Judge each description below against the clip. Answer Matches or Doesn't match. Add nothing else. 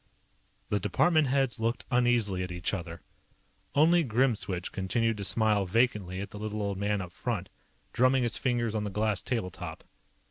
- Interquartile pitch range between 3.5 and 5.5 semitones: Matches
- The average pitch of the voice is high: Doesn't match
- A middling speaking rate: Matches